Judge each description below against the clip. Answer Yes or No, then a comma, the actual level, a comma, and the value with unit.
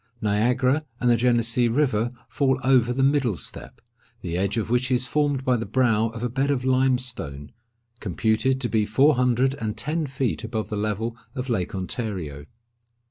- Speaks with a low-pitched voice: Yes, low, 120 Hz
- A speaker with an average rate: Yes, average, 175 wpm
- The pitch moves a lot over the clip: No, average, 3.3 semitones